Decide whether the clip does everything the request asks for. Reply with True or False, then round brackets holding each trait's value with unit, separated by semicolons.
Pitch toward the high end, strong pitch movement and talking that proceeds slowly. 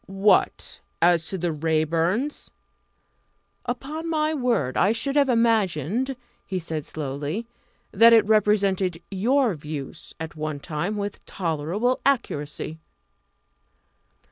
True (195 Hz; 6.6 semitones; 110 wpm)